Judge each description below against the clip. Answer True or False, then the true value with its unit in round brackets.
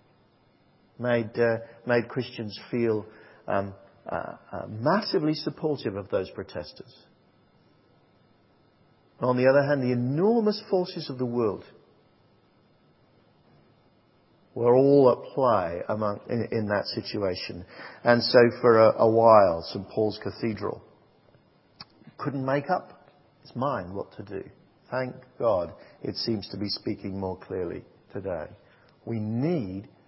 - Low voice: True (120 Hz)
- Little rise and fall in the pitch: False (4.4 semitones)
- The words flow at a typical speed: False (125 wpm)